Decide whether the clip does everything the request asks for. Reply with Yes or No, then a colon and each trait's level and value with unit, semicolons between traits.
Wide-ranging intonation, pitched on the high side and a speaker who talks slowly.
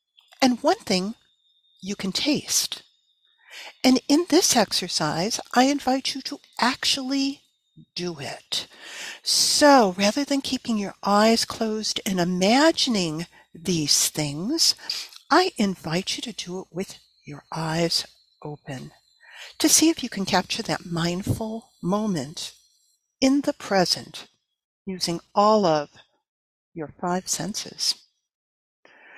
Yes: wide, 7.3 semitones; high, 200 Hz; slow, 115 wpm